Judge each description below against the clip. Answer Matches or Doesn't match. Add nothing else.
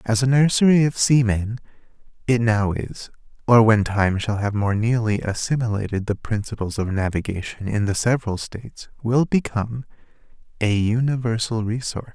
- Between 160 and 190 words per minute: Doesn't match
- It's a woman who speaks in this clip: Doesn't match